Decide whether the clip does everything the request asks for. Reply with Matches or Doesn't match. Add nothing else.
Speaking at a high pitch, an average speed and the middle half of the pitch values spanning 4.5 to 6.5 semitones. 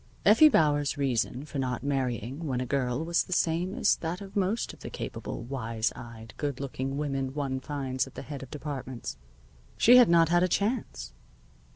Doesn't match